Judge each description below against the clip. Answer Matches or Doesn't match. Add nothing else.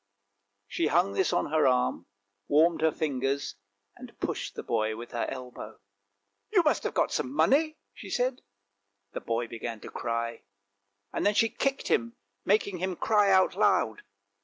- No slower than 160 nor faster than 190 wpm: Matches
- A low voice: Doesn't match